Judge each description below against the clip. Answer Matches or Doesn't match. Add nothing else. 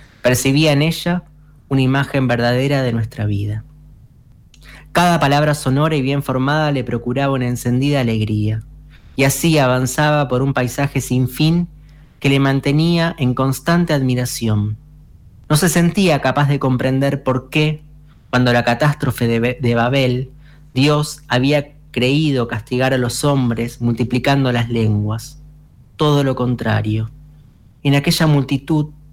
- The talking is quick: Doesn't match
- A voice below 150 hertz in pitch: Matches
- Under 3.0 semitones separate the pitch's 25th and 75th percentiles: Doesn't match